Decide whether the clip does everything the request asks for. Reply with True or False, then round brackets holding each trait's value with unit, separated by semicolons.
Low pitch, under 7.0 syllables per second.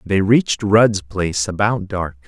True (100 Hz; 4.3 syllables/s)